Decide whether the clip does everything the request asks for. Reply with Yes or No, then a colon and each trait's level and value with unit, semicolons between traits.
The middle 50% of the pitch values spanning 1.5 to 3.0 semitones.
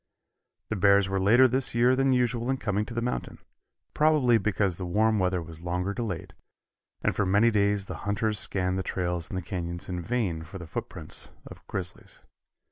No: average, 4.4 semitones